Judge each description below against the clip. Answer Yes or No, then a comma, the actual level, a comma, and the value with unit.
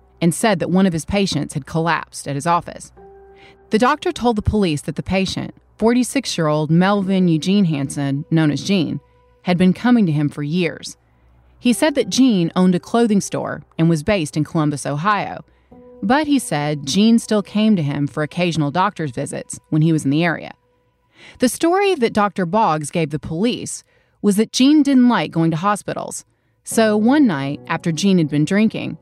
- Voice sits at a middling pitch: Yes, medium, 180 Hz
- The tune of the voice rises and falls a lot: Yes, wide, 6.4 semitones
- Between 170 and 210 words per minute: Yes, average, 190 wpm